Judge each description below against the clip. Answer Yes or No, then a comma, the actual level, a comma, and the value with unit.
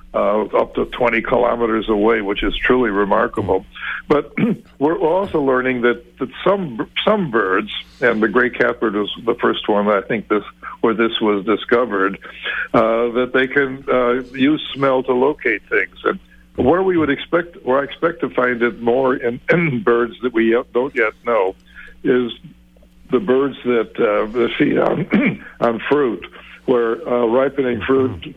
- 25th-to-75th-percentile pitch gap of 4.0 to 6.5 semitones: No, average, 2.7 semitones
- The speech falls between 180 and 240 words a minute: No, average, 165 wpm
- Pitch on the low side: Yes, low, 120 Hz